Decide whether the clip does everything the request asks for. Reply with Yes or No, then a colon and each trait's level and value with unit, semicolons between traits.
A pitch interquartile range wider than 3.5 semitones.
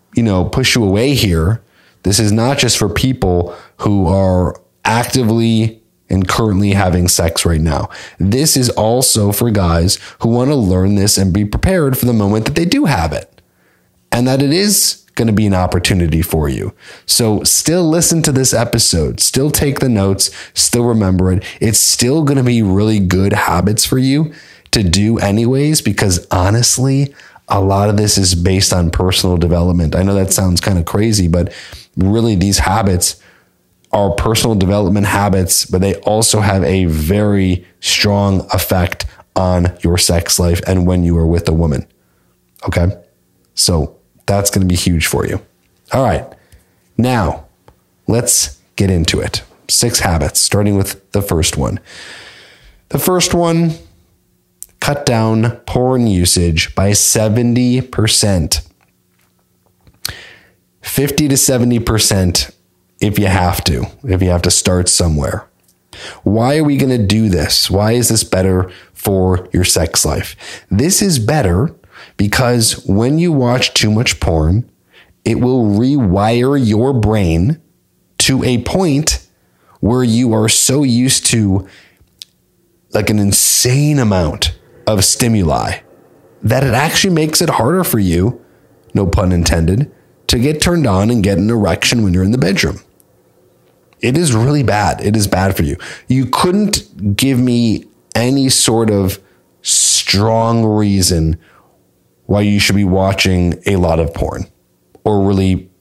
Yes: average, 4.8 semitones